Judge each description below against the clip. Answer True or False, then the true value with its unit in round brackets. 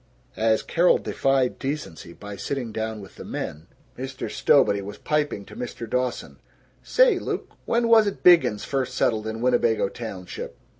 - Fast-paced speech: False (150 wpm)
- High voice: False (120 Hz)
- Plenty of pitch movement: False (4.7 semitones)